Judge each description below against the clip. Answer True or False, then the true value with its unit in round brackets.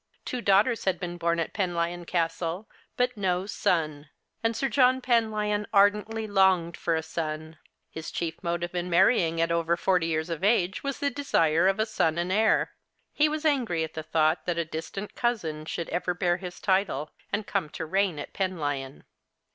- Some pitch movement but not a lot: True (4.2 semitones)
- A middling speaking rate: True (185 wpm)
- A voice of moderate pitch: True (180 Hz)